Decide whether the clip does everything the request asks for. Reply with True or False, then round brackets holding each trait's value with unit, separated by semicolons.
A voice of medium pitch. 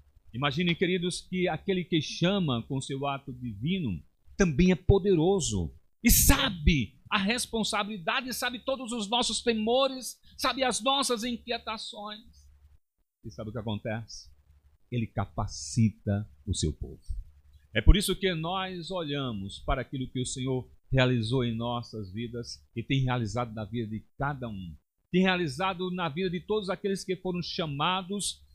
True (145 Hz)